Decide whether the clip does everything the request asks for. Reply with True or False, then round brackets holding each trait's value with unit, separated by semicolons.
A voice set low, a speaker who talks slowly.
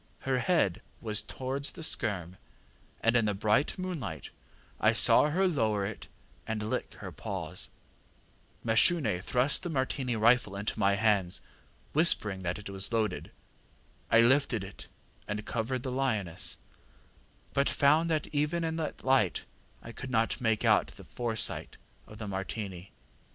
False (115 Hz; 145 wpm)